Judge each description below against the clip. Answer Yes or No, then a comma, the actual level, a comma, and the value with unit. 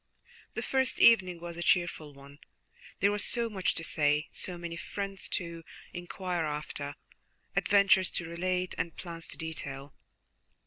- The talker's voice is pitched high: No, medium, 170 Hz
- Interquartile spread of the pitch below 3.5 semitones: Yes, average, 2.9 semitones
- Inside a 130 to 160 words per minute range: Yes, average, 145 wpm